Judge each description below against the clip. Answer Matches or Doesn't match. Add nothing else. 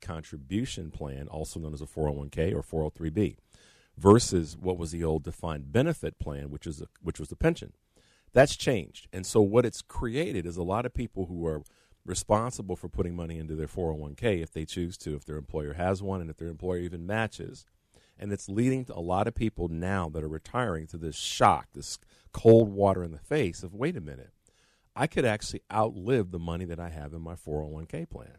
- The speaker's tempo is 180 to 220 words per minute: Matches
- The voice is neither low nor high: Doesn't match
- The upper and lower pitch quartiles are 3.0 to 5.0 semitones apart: Matches